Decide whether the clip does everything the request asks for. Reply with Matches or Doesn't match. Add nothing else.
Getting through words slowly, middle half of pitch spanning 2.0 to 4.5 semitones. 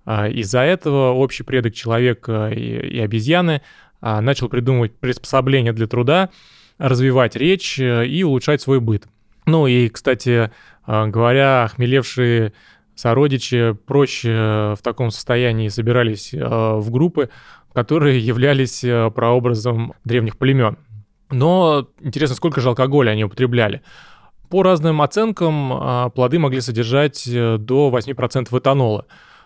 Matches